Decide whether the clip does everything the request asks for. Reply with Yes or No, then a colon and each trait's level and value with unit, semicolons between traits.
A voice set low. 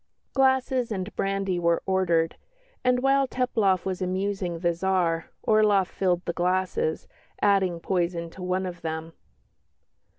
No: medium, 185 Hz